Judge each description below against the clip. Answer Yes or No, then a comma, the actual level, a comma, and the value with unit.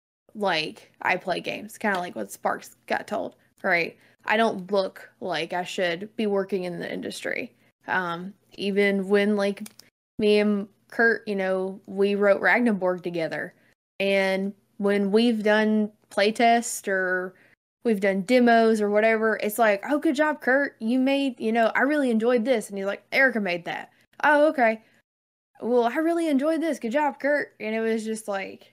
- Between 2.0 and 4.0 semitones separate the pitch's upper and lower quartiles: Yes, average, 3.3 semitones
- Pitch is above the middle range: Yes, high, 215 Hz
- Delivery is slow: No, average, 170 wpm